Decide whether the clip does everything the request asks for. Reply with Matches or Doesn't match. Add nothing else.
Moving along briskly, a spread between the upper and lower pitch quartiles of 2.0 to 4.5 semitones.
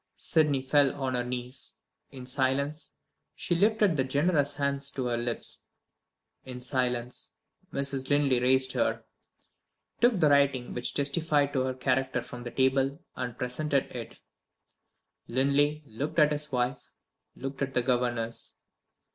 Doesn't match